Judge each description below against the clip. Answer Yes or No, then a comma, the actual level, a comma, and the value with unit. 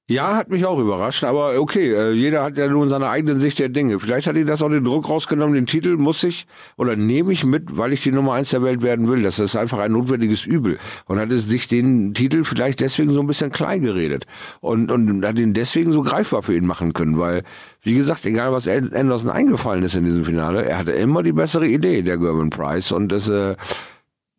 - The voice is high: No, low, 125 Hz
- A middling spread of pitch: No, wide, 5.9 semitones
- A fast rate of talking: Yes, fast, 230 wpm